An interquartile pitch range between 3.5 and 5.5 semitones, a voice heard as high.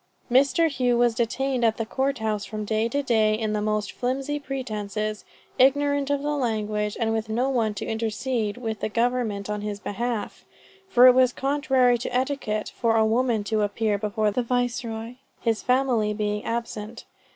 No: average, 3.0 semitones; high, 230 Hz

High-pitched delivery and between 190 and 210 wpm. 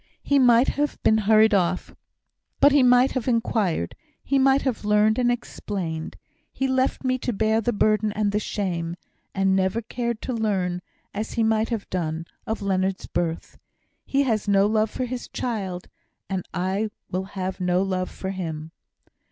No: high, 210 Hz; average, 170 wpm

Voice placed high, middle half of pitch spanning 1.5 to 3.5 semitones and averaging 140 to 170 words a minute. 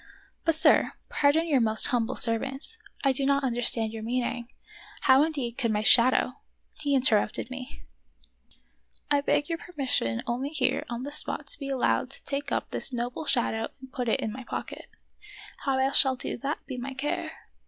No: very high, 260 Hz; average, 3.1 semitones; average, 195 wpm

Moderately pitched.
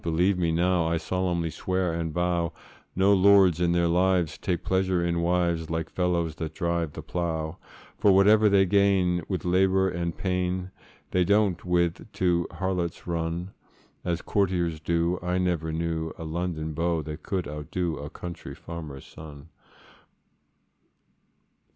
No: very low, 85 Hz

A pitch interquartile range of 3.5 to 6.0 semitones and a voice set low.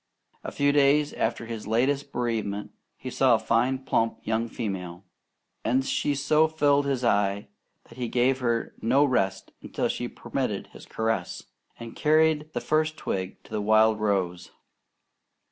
Yes: average, 4.6 semitones; low, 120 Hz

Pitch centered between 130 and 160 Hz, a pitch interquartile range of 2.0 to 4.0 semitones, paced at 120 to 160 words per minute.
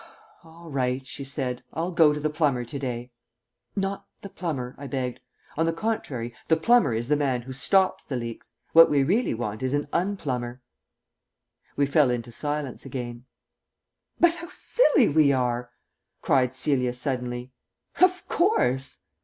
No: low, 135 Hz; average, 4.7 semitones; average, 155 wpm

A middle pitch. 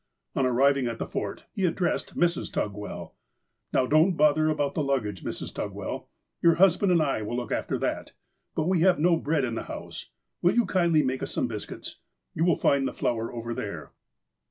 Yes: medium, 145 Hz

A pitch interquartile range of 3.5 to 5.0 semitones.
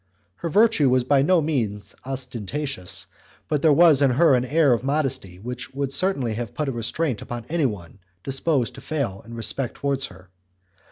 Yes: average, 4.2 semitones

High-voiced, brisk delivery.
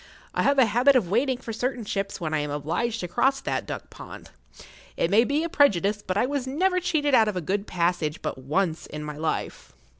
Yes: high, 210 Hz; fast, 230 wpm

